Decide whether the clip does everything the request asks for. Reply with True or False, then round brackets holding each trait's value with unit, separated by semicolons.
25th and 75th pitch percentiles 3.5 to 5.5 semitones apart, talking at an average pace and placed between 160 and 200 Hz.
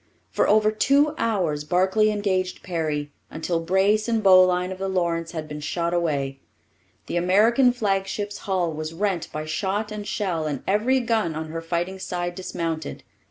True (4.0 semitones; 160 wpm; 185 Hz)